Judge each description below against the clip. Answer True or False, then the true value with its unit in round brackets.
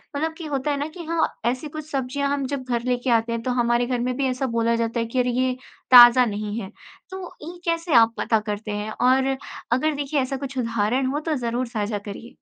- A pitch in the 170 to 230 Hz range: False (255 Hz)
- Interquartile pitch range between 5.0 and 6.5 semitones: False (3.4 semitones)